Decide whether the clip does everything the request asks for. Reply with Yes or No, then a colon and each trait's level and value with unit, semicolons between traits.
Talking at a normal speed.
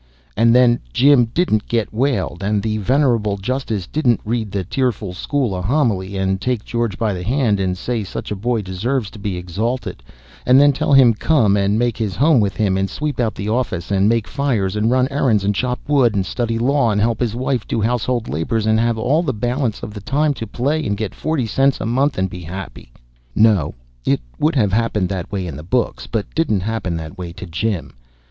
No: fast, 220 wpm